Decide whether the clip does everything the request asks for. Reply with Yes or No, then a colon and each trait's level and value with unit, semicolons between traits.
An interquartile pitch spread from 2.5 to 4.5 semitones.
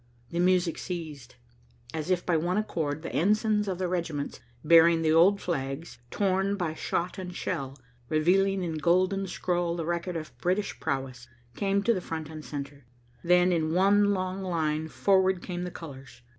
Yes: average, 3.1 semitones